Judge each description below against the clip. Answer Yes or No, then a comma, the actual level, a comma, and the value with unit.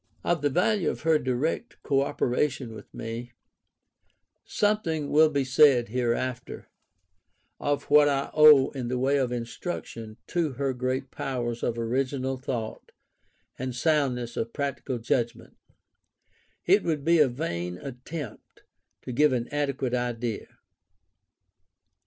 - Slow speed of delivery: Yes, slow, 125 wpm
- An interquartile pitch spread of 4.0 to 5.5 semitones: No, average, 3.3 semitones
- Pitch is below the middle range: Yes, low, 130 Hz